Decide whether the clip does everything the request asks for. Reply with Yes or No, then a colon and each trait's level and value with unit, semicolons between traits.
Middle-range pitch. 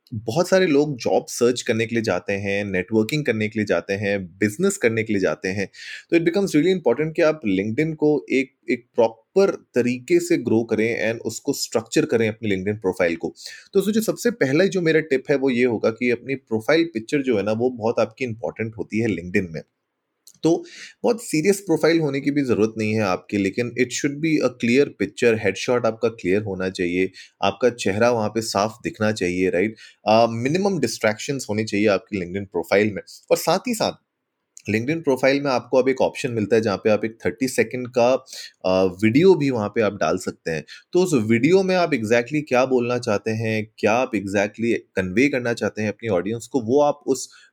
No: low, 120 Hz